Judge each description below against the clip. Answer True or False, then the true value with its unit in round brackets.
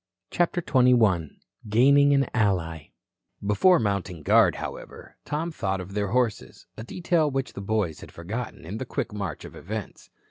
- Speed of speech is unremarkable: True (155 wpm)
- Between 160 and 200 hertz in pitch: False (110 Hz)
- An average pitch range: False (5.9 semitones)